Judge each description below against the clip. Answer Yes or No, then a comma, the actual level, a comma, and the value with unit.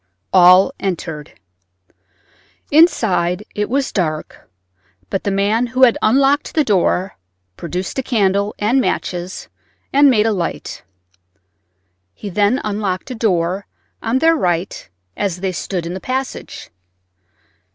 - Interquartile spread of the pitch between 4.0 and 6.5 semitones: Yes, wide, 5.4 semitones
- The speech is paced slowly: Yes, slow, 125 wpm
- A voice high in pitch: Yes, high, 200 Hz